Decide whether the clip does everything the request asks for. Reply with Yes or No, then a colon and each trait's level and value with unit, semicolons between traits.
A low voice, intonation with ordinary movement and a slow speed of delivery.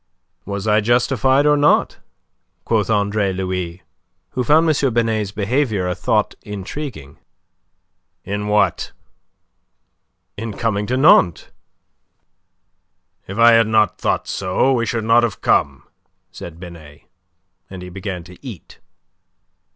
Yes: low, 105 Hz; average, 4.1 semitones; slow, 120 wpm